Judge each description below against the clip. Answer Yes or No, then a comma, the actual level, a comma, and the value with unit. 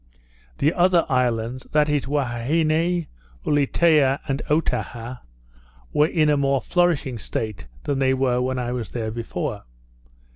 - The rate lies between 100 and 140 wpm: Yes, slow, 135 wpm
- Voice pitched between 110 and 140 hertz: Yes, low, 135 Hz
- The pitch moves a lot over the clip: No, average, 3.8 semitones